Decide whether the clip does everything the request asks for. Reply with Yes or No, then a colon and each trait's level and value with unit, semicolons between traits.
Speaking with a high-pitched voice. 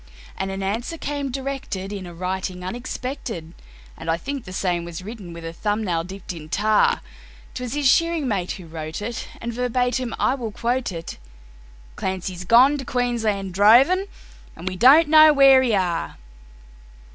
Yes: high, 215 Hz